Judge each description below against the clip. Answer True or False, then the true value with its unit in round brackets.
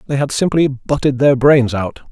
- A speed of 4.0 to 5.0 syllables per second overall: True (4.8 syllables/s)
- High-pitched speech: False (135 Hz)